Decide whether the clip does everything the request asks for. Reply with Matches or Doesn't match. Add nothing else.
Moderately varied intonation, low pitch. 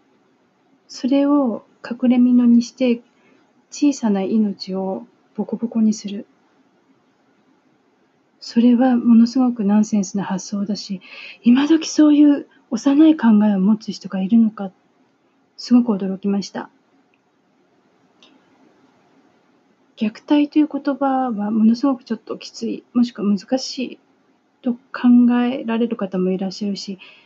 Doesn't match